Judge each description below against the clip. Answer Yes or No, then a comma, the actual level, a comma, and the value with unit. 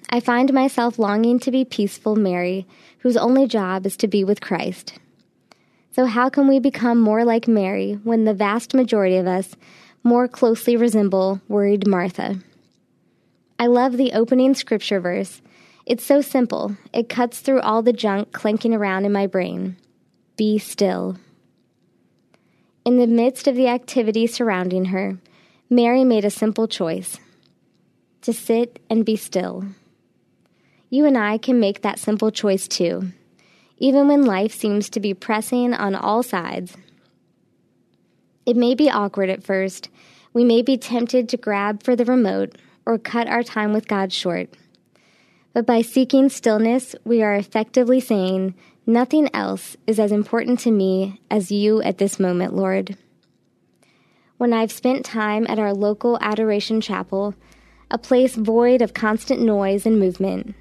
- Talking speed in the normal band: Yes, average, 150 wpm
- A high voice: Yes, high, 220 Hz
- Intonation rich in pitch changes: No, average, 3.4 semitones